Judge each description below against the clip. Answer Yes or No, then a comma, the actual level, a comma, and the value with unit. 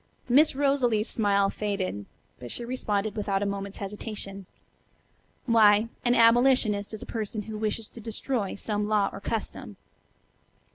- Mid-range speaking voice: No, high, 215 Hz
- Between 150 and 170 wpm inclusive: No, average, 140 wpm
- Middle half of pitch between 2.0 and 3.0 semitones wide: Yes, narrow, 2.4 semitones